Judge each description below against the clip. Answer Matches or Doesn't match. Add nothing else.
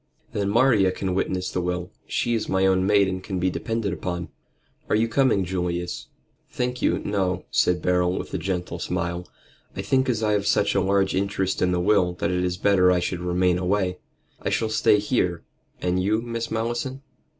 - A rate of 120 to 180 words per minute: Doesn't match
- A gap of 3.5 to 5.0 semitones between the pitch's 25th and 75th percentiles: Doesn't match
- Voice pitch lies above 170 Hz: Doesn't match